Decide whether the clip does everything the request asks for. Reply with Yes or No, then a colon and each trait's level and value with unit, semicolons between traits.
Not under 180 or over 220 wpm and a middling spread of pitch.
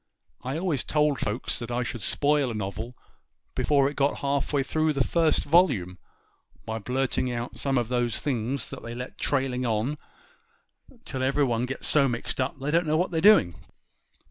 Yes: average, 185 wpm; average, 3.6 semitones